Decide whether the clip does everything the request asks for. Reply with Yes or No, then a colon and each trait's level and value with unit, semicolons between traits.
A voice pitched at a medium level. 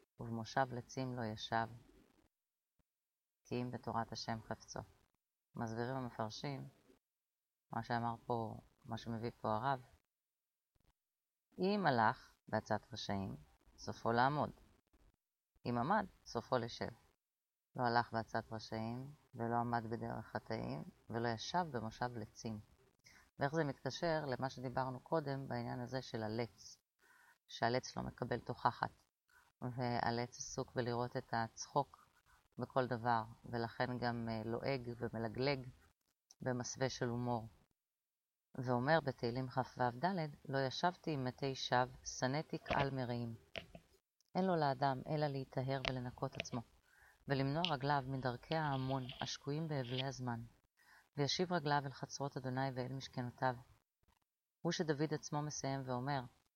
No: low, 125 Hz